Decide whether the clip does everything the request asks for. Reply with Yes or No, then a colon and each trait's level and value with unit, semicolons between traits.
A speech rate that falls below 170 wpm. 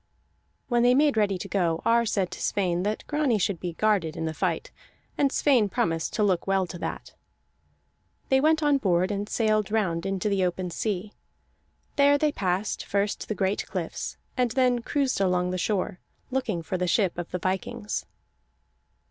No: average, 180 wpm